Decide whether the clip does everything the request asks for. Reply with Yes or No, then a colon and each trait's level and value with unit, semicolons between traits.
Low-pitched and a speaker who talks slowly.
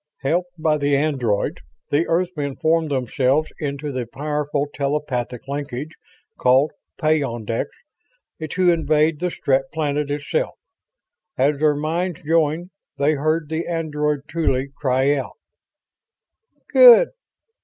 No: medium, 150 Hz; slow, 110 wpm